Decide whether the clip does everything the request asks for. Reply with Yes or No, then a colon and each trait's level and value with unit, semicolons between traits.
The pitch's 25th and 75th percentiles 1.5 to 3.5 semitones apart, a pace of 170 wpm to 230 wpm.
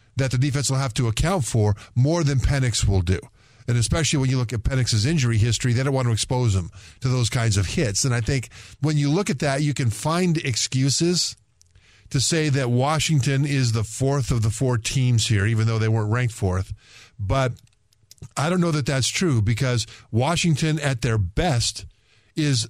No: average, 4.0 semitones; average, 200 wpm